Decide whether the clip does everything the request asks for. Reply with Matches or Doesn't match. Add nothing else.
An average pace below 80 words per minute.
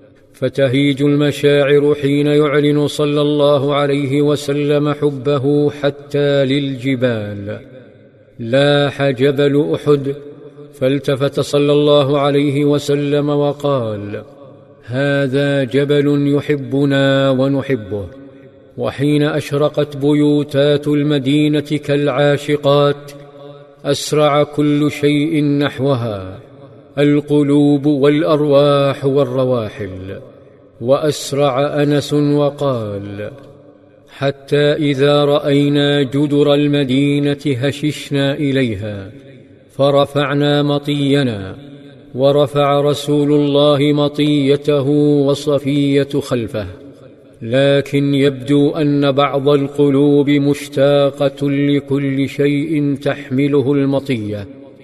Matches